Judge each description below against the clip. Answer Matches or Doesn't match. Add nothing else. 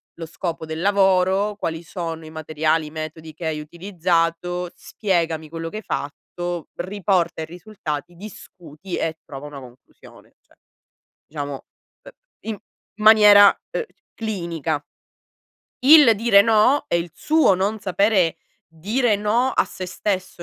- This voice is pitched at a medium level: Matches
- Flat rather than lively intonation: Doesn't match